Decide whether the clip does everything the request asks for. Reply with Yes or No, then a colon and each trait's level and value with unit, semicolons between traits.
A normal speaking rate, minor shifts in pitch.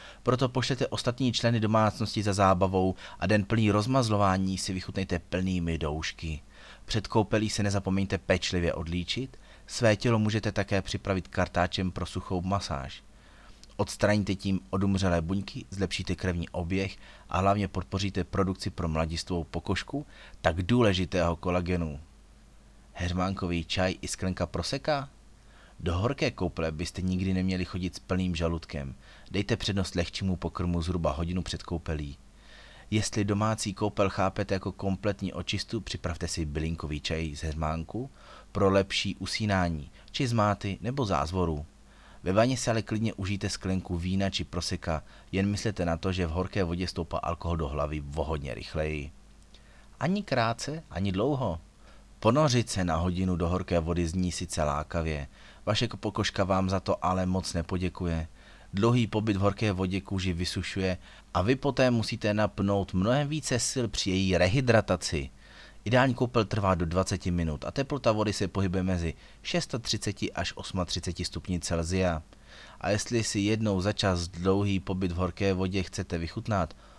No: average, 145 wpm; average, 3.2 semitones